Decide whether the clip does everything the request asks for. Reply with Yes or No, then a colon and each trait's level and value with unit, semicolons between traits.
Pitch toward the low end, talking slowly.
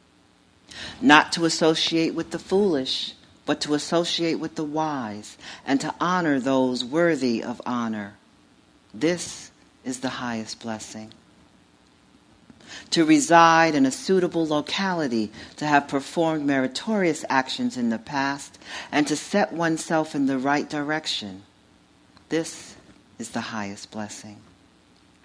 No: medium, 145 Hz; slow, 120 wpm